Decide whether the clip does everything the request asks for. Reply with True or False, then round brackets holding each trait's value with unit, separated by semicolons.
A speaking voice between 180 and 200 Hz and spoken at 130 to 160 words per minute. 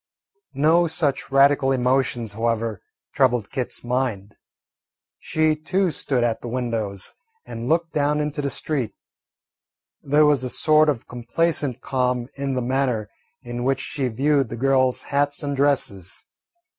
False (135 Hz; 140 wpm)